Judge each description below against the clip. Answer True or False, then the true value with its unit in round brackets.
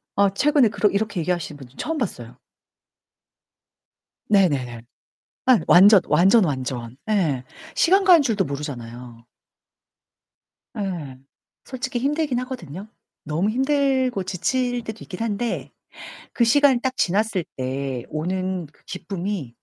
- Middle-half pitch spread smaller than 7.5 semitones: False (8.7 semitones)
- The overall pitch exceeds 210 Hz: False (195 Hz)